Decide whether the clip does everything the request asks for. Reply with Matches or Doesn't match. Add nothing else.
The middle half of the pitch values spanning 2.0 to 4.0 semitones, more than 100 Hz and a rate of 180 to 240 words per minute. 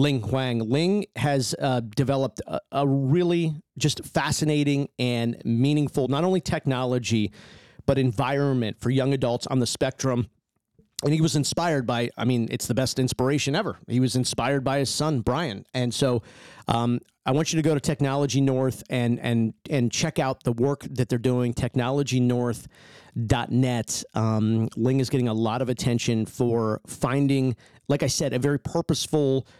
Doesn't match